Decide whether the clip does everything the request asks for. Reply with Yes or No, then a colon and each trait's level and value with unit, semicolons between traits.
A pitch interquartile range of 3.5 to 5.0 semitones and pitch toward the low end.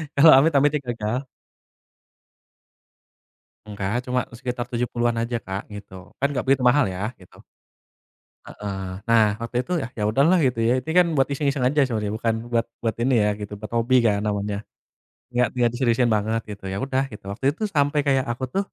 Yes: average, 4.0 semitones; low, 120 Hz